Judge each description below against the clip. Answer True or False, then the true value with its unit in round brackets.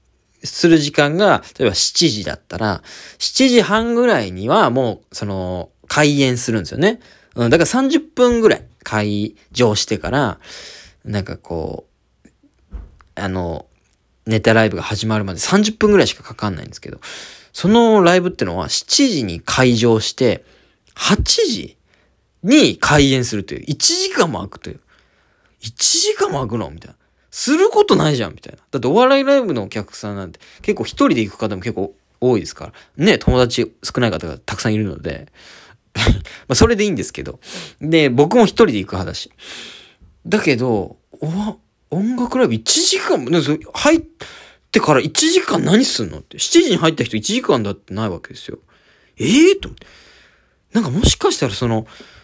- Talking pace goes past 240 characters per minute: True (310 characters per minute)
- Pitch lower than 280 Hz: True (140 Hz)